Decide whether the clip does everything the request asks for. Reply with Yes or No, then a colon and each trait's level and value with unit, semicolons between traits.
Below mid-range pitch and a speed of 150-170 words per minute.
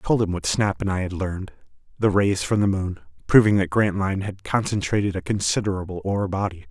No: very low, 95 Hz; fast, 205 wpm